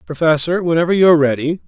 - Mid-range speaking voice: Yes, medium, 160 Hz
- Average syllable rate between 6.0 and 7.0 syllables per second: Yes, 6.7 syllables/s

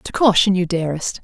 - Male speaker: No, female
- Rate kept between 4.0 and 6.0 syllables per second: Yes, 5.9 syllables/s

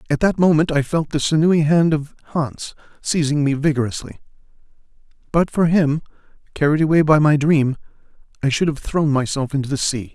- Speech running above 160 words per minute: Yes, average, 170 wpm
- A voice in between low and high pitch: Yes, medium, 150 Hz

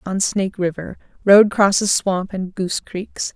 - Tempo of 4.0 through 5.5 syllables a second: Yes, 4.4 syllables/s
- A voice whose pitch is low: No, high, 195 Hz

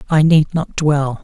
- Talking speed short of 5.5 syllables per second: Yes, 3.9 syllables/s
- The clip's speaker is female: No, male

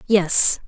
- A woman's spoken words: Yes, female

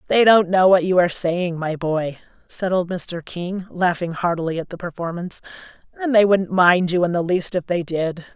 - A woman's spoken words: Yes, female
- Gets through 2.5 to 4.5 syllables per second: No, 5.0 syllables/s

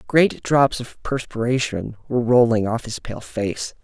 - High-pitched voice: No, low, 120 Hz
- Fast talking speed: No, average, 155 wpm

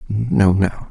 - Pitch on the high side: No, low, 100 Hz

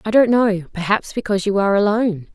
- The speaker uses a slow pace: No, fast, 205 wpm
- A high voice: Yes, high, 205 Hz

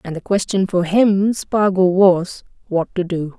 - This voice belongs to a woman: Yes, female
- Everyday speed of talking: Yes, average, 160 wpm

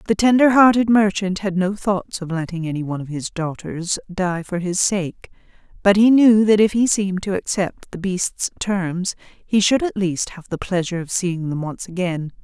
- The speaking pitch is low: No, high, 190 Hz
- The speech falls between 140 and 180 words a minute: No, fast, 205 wpm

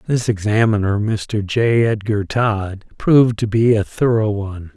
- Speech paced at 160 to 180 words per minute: No, average, 150 wpm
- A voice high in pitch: No, low, 110 Hz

